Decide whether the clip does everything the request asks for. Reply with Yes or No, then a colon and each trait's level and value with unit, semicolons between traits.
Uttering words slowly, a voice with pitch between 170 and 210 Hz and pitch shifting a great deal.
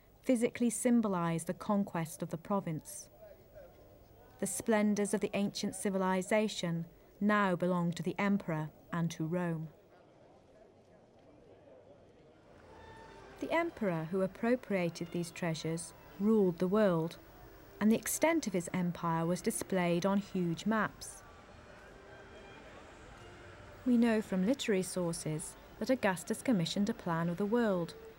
No: slow, 115 wpm; high, 190 Hz; average, 4.0 semitones